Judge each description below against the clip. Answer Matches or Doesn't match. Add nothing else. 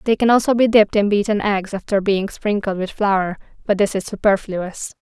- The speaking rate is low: Doesn't match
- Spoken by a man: Doesn't match